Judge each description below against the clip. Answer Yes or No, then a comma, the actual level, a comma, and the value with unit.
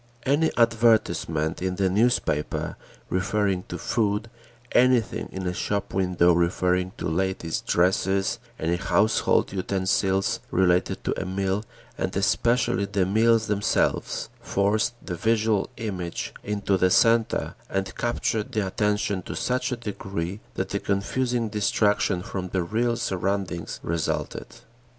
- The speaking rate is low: Yes, slow, 125 wpm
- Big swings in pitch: No, average, 3.2 semitones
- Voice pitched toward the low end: Yes, low, 100 Hz